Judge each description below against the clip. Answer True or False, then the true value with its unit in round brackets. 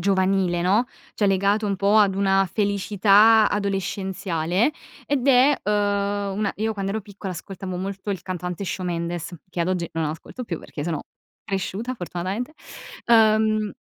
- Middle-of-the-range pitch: False (195 Hz)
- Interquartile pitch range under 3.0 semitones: True (2.5 semitones)